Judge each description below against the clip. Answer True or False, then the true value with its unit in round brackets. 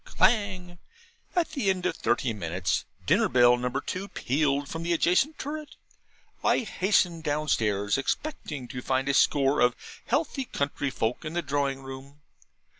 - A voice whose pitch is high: False (145 Hz)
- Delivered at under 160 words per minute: True (150 wpm)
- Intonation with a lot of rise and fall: True (5.9 semitones)